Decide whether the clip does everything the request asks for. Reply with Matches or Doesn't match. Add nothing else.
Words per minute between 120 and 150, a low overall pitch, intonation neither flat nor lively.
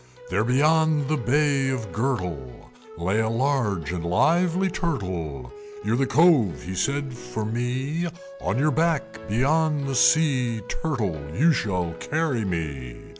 Doesn't match